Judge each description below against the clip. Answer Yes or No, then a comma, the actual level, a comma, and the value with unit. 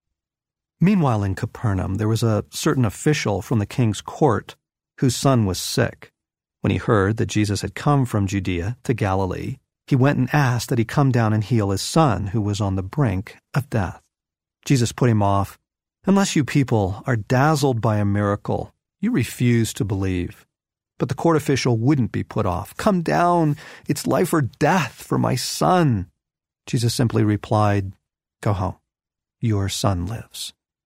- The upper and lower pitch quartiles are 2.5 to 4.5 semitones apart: No, average, 5.2 semitones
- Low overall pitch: Yes, low, 115 Hz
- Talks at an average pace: Yes, average, 170 wpm